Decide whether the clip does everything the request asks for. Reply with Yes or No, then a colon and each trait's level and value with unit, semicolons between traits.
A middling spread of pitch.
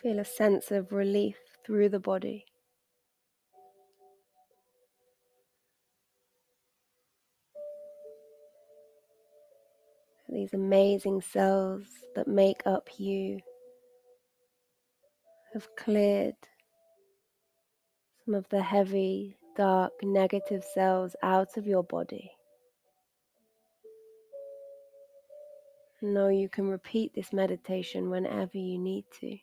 No: wide, 7.3 semitones